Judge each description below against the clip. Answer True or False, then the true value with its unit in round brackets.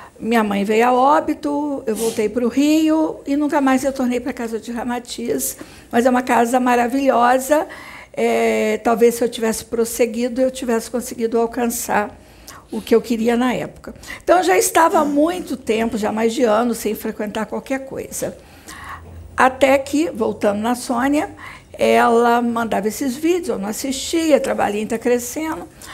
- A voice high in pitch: True (245 Hz)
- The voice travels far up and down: False (3.1 semitones)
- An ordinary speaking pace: True (160 wpm)